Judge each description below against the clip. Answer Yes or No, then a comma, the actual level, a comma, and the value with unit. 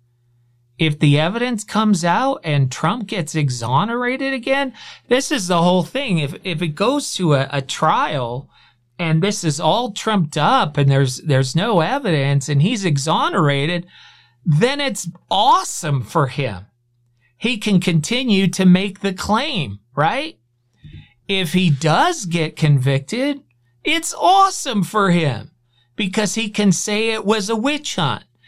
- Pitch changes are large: Yes, wide, 7.5 semitones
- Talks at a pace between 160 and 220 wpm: No, average, 145 wpm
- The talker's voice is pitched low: No, medium, 175 Hz